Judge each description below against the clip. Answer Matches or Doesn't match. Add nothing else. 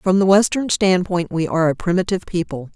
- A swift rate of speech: Doesn't match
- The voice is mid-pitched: Matches